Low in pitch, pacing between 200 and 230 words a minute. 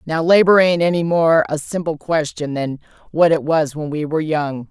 No: medium, 160 Hz; fast, 205 wpm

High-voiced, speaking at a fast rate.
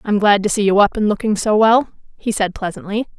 Yes: high, 210 Hz; fast, 245 wpm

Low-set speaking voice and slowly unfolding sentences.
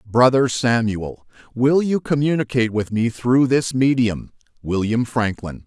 Yes: low, 120 Hz; slow, 115 wpm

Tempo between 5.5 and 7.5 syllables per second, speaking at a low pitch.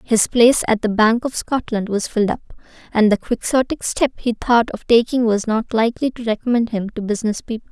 No: 5.7 syllables/s; high, 225 Hz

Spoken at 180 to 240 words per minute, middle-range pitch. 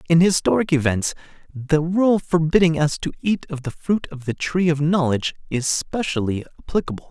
No: average, 170 wpm; medium, 160 Hz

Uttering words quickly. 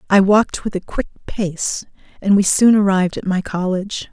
No: average, 190 wpm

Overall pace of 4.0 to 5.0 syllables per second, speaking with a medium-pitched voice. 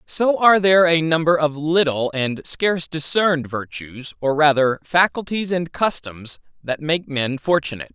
Yes: 4.7 syllables/s; medium, 150 Hz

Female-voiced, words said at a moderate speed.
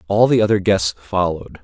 No: male; average, 185 wpm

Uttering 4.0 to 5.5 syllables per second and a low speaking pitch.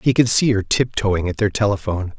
No: 5.8 syllables/s; low, 105 Hz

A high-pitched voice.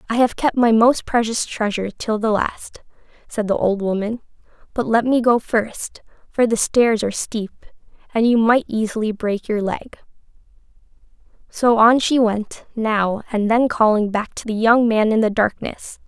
Yes: high, 225 Hz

